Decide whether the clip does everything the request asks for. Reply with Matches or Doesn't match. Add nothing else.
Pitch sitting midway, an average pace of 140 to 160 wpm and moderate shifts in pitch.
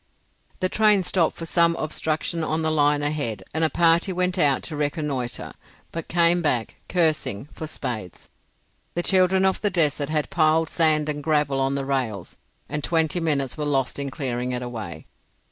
Doesn't match